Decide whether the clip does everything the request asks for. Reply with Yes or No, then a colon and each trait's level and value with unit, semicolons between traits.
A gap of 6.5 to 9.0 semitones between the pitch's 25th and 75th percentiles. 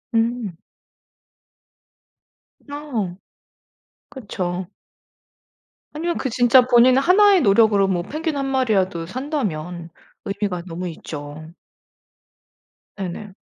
Yes: wide, 7.1 semitones